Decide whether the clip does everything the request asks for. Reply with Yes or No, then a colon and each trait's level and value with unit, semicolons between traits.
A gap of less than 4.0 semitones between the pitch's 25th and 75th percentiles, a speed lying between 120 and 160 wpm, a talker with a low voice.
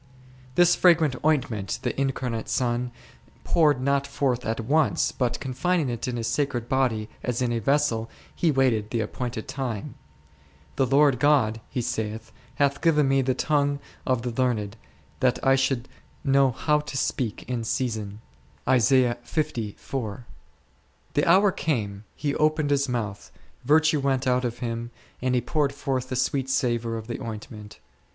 Yes: average, 3.5 semitones; average, 150 wpm; low, 130 Hz